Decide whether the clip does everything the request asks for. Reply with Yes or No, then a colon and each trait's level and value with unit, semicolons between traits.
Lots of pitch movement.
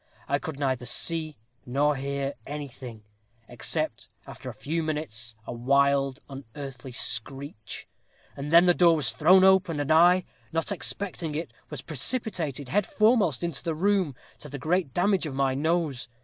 No: average, 4.1 semitones